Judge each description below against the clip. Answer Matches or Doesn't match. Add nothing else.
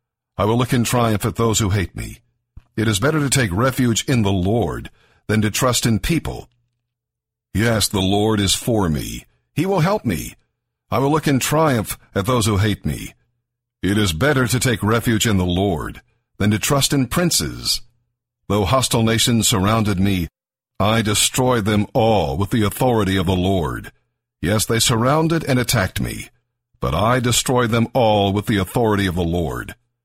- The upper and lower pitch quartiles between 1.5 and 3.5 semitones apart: Matches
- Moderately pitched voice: Doesn't match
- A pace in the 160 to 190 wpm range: Matches